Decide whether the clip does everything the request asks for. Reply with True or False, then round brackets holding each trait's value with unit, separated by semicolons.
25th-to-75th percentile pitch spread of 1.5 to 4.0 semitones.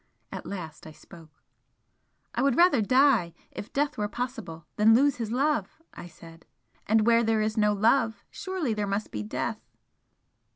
False (4.6 semitones)